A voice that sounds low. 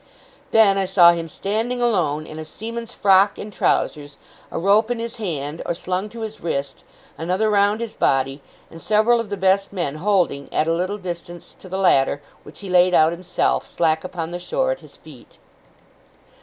No: medium, 185 Hz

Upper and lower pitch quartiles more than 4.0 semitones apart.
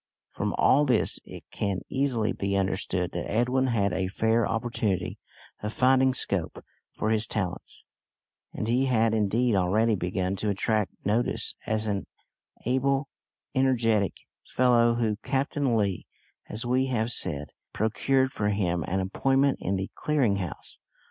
Yes: average, 4.4 semitones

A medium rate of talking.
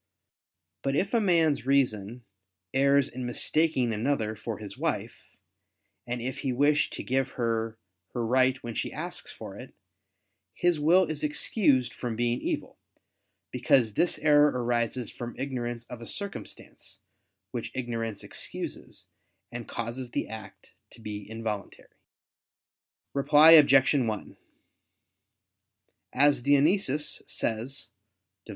No: slow, 125 wpm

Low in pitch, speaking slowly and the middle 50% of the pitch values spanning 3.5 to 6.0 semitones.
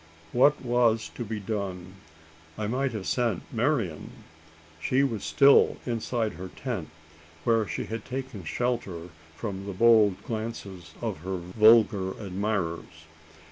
Yes: low, 110 Hz; slow, 130 wpm; average, 3.9 semitones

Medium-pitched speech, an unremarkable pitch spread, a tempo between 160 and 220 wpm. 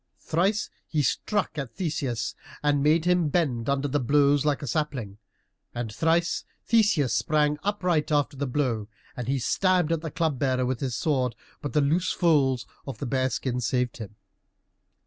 Yes: medium, 145 Hz; average, 4.2 semitones; average, 170 wpm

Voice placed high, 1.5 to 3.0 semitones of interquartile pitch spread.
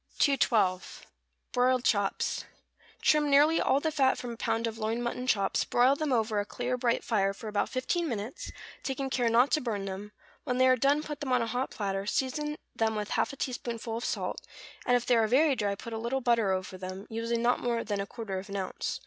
No: high, 235 Hz; average, 3.6 semitones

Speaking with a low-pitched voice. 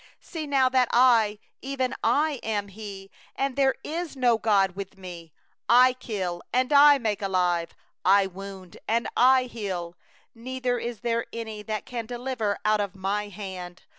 No: high, 220 Hz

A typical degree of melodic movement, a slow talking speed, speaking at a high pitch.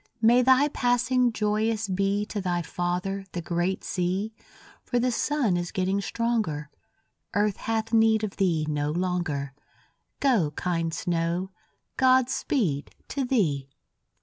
Yes: average, 4.9 semitones; slow, 130 wpm; high, 195 Hz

